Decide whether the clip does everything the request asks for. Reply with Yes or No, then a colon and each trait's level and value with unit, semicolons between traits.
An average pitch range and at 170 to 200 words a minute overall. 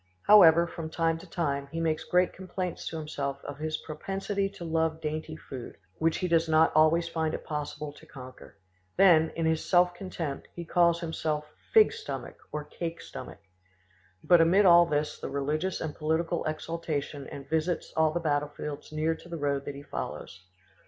No: narrow, 2.2 semitones; average, 180 wpm